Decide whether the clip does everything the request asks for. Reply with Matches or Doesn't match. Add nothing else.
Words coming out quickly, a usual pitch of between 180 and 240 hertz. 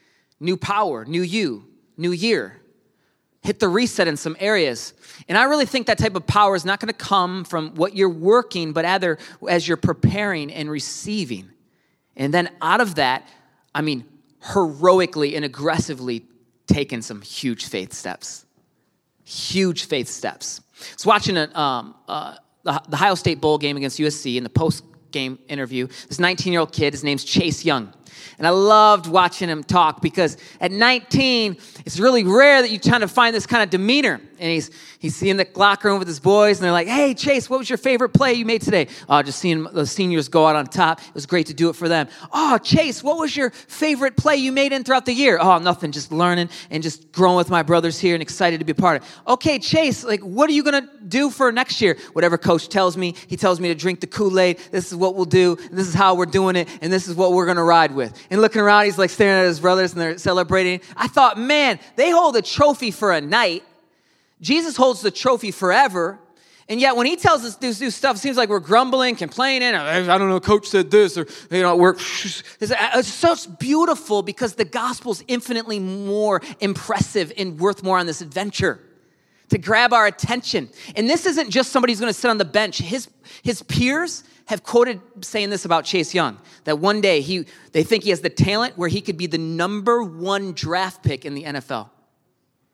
Matches